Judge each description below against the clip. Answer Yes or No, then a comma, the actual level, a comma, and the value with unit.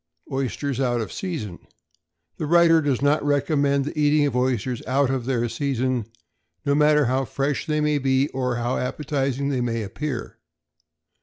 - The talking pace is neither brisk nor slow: Yes, average, 160 wpm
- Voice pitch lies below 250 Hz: Yes, low, 135 Hz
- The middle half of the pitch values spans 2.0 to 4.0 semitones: Yes, narrow, 2.6 semitones